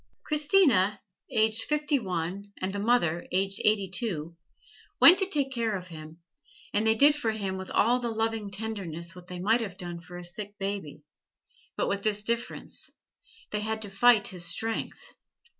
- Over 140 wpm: Yes, average, 175 wpm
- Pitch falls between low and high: No, high, 205 Hz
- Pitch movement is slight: No, average, 3.8 semitones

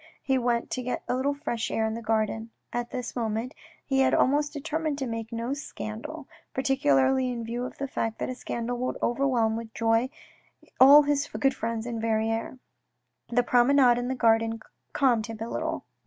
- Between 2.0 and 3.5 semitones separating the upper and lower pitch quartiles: Yes, average, 2.9 semitones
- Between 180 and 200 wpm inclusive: Yes, average, 185 wpm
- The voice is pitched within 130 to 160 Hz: No, high, 240 Hz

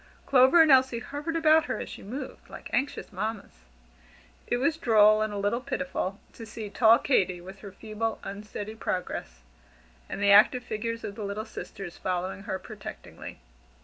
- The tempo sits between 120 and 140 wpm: No, average, 170 wpm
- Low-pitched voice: No, high, 215 Hz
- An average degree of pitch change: Yes, average, 4.3 semitones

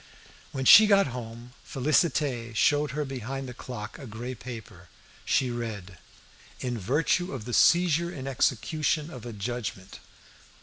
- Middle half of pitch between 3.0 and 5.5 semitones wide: Yes, average, 4.3 semitones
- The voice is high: No, low, 125 Hz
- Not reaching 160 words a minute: Yes, average, 140 wpm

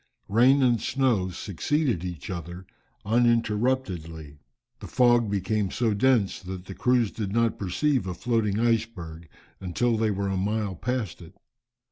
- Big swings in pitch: No, average, 4.5 semitones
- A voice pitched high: No, low, 105 Hz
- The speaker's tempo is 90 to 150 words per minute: Yes, average, 145 wpm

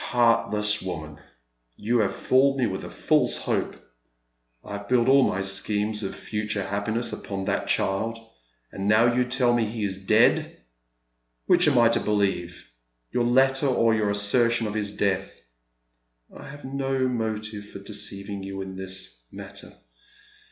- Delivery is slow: No, average, 160 wpm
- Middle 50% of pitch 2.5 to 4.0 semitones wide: Yes, average, 3.6 semitones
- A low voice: Yes, low, 105 Hz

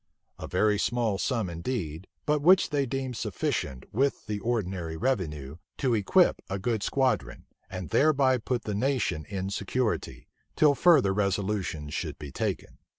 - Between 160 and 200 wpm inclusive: No, average, 150 wpm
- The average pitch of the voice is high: No, low, 105 Hz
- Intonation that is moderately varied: No, wide, 6.0 semitones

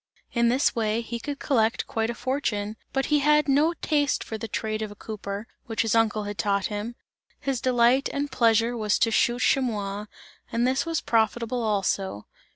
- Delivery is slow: No, average, 185 wpm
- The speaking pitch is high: Yes, high, 230 Hz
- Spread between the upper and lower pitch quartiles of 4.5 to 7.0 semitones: No, average, 3.4 semitones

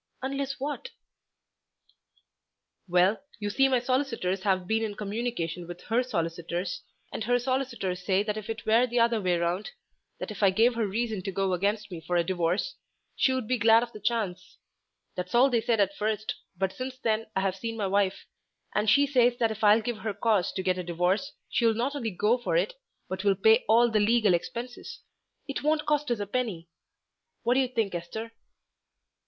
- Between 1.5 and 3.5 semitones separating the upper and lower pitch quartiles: No, average, 4.2 semitones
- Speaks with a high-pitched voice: Yes, high, 220 Hz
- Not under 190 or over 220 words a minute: Yes, average, 195 wpm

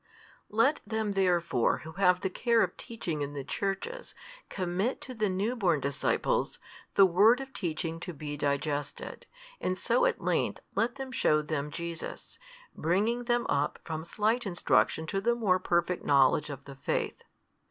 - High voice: No, medium, 180 Hz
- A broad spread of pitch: Yes, wide, 6.4 semitones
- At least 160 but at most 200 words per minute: Yes, average, 165 wpm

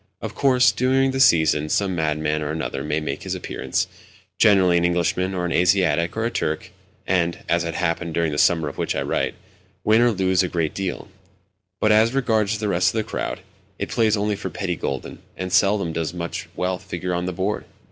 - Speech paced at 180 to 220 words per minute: Yes, average, 200 wpm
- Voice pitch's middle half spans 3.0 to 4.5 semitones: Yes, average, 4.1 semitones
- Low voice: Yes, very low, 90 Hz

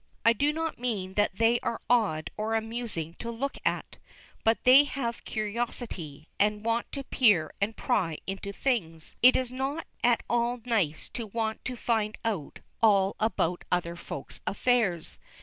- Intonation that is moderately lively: Yes, average, 3.9 semitones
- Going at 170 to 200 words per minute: No, average, 160 wpm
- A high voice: Yes, high, 225 Hz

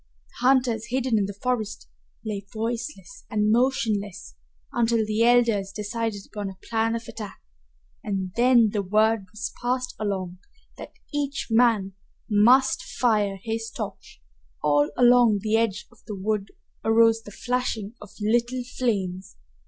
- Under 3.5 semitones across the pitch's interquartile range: Yes, average, 2.9 semitones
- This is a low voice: No, high, 225 Hz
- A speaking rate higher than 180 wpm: No, average, 140 wpm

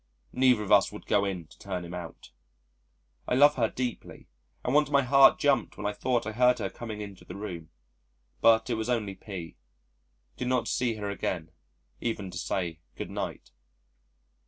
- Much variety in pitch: No, average, 4.8 semitones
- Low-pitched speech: Yes, low, 110 Hz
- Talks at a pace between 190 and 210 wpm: No, average, 180 wpm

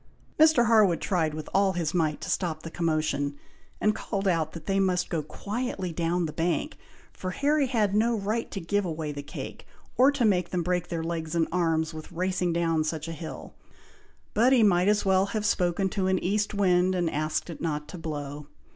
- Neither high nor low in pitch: Yes, medium, 180 Hz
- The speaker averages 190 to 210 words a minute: Yes, fast, 205 wpm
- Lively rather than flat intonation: No, average, 3.8 semitones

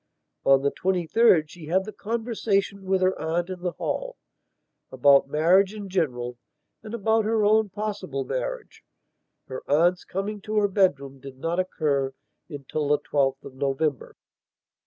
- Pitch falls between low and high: Yes, medium, 180 Hz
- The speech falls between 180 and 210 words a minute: No, average, 145 wpm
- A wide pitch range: Yes, wide, 6.4 semitones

